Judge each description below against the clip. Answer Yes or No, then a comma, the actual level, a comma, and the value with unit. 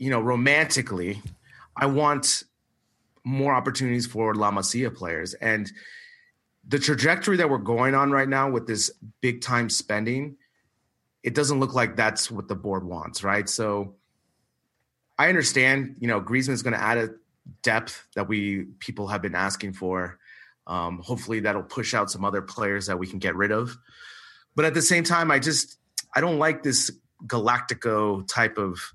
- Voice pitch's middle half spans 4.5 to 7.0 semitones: Yes, average, 5.1 semitones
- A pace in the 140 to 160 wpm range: No, average, 170 wpm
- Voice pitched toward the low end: Yes, low, 120 Hz